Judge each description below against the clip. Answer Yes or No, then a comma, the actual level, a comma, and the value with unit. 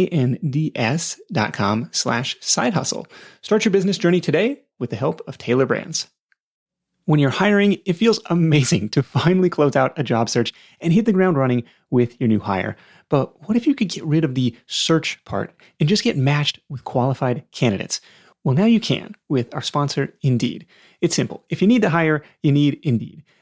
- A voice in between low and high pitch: Yes, medium, 155 Hz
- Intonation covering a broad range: Yes, wide, 5.7 semitones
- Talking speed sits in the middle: Yes, average, 185 wpm